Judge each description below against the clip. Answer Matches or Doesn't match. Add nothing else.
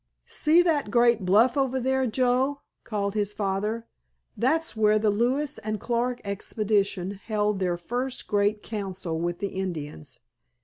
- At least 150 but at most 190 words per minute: Doesn't match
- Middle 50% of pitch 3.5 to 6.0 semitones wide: Matches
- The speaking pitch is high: Matches